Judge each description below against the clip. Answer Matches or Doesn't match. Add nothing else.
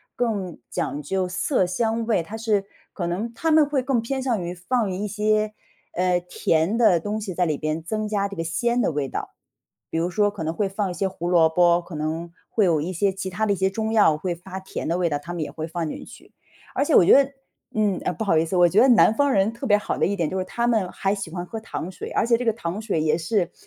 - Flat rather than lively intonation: Doesn't match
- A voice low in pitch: Doesn't match